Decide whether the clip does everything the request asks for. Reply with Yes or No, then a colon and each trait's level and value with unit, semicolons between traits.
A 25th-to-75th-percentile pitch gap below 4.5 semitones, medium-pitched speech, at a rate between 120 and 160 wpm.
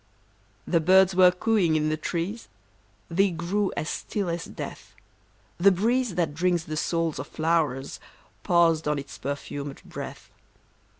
Yes: average, 3.2 semitones; medium, 170 Hz; average, 140 wpm